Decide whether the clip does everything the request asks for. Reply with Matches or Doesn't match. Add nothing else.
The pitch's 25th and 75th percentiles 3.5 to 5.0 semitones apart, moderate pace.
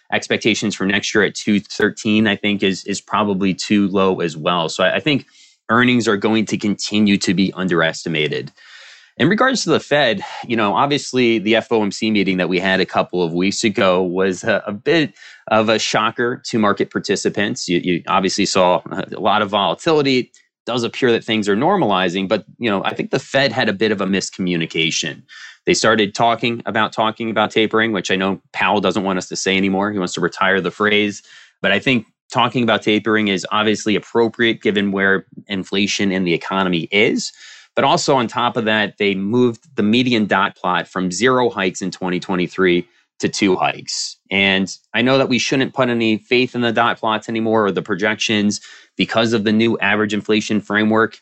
Doesn't match